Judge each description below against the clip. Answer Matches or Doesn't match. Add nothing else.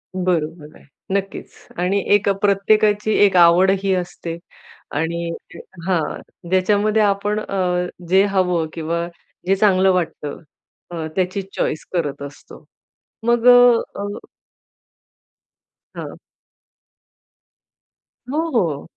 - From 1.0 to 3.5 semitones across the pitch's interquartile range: Matches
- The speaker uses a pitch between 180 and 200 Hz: Matches